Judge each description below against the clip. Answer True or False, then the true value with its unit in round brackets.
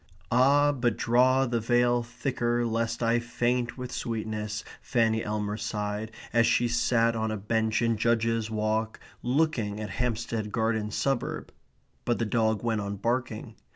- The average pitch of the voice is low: True (115 Hz)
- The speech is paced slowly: False (150 wpm)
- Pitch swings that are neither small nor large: False (1.7 semitones)